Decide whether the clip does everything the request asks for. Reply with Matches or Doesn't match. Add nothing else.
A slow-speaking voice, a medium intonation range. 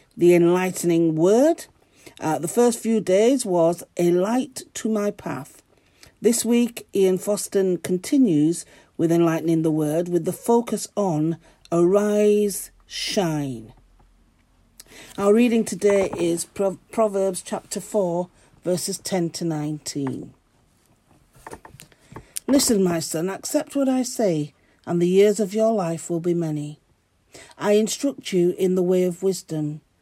Matches